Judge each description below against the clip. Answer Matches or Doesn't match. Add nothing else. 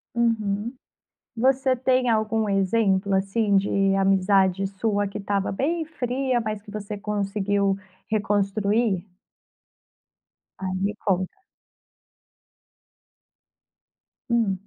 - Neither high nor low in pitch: Doesn't match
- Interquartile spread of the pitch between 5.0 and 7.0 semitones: Doesn't match